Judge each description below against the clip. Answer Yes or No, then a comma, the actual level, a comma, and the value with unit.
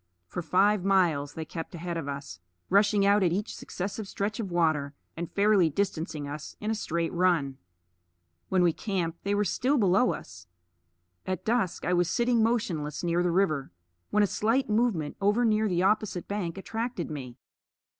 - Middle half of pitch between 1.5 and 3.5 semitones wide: No, average, 4.3 semitones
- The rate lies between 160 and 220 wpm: Yes, average, 175 wpm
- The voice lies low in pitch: No, medium, 185 Hz